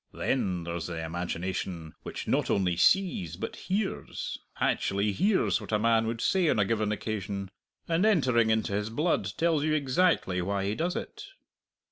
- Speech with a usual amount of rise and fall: No, wide, 8.7 semitones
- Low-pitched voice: Yes, low, 110 Hz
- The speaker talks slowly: No, average, 165 wpm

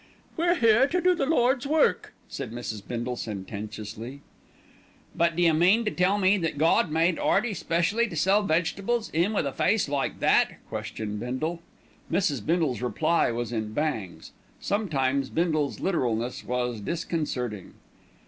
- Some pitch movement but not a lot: No, wide, 8.3 semitones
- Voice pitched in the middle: Yes, medium, 160 Hz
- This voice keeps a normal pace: Yes, average, 145 wpm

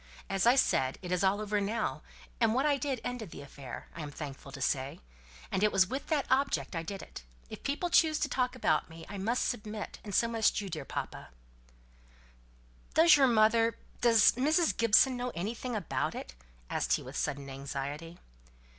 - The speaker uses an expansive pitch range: Yes, wide, 7.4 semitones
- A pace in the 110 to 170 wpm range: No, average, 185 wpm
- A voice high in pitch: Yes, high, 215 Hz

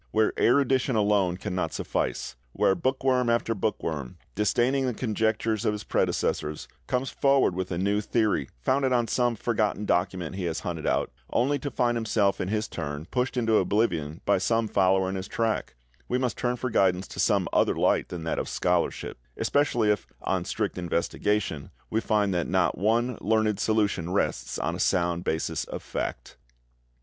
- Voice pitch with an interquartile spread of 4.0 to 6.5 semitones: Yes, average, 4.5 semitones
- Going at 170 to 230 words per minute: Yes, average, 175 wpm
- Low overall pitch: Yes, low, 105 Hz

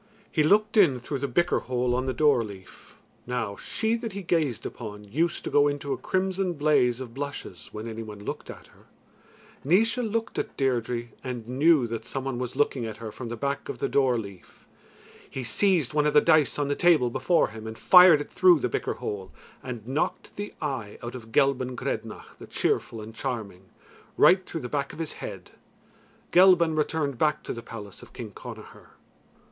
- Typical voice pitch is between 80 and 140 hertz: Yes, low, 135 Hz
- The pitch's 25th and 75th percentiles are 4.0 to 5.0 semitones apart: No, wide, 5.4 semitones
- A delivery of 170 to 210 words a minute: Yes, average, 200 wpm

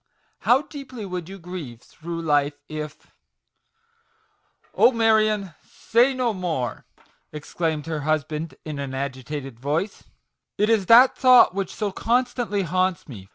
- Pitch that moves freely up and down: Yes, wide, 7.0 semitones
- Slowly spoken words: No, average, 150 wpm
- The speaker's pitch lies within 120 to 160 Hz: No, medium, 180 Hz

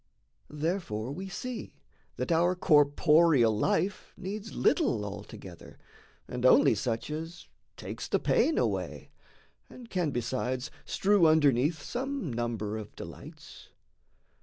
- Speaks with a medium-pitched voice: Yes, medium, 150 Hz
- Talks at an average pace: No, slow, 110 wpm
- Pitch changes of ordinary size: No, wide, 7.1 semitones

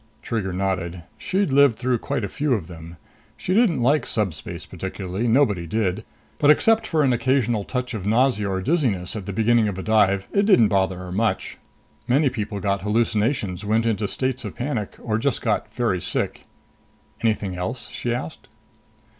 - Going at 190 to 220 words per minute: No, average, 175 wpm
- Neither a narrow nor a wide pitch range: Yes, average, 4.9 semitones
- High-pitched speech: No, low, 110 Hz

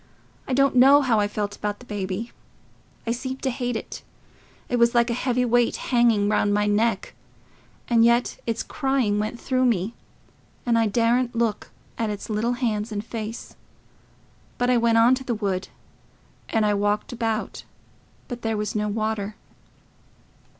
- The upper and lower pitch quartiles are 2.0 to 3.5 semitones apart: Yes, average, 2.7 semitones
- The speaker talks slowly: No, average, 165 wpm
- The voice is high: Yes, high, 230 Hz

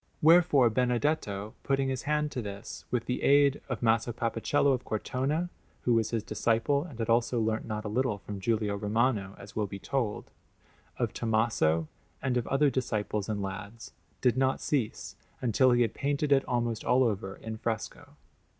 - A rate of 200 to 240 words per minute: No, average, 175 wpm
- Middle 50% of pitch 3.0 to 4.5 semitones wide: Yes, average, 3.6 semitones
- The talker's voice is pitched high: No, low, 115 Hz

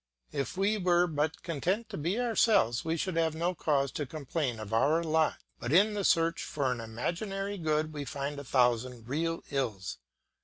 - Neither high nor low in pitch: Yes, medium, 155 Hz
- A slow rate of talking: No, average, 185 wpm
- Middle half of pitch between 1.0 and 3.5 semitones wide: No, average, 4.6 semitones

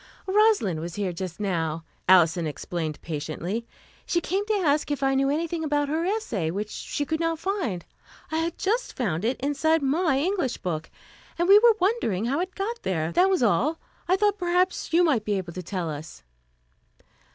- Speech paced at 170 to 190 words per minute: Yes, average, 185 wpm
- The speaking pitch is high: Yes, very high, 280 Hz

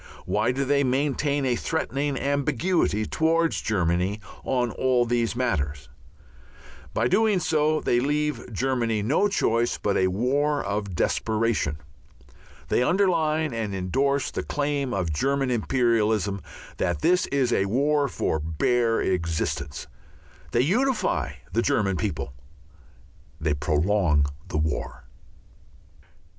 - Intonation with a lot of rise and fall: Yes, wide, 6.4 semitones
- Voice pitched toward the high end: No, low, 120 Hz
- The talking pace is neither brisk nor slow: No, slow, 120 wpm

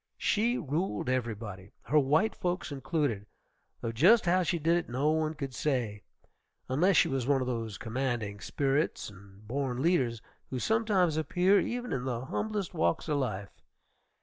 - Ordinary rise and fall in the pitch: No, wide, 6.7 semitones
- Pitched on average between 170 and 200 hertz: No, low, 135 Hz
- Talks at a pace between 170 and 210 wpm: No, average, 160 wpm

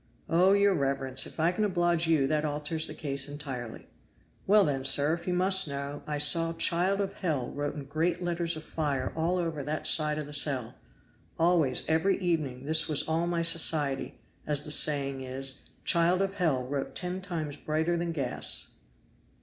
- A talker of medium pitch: Yes, medium, 155 Hz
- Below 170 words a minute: No, average, 180 wpm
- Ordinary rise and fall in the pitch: Yes, average, 3.5 semitones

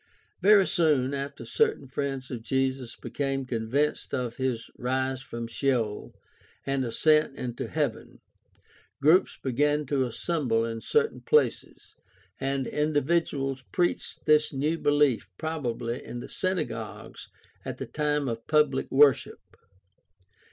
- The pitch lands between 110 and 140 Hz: Yes, low, 135 Hz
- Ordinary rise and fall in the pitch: Yes, average, 3.2 semitones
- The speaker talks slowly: Yes, slow, 125 wpm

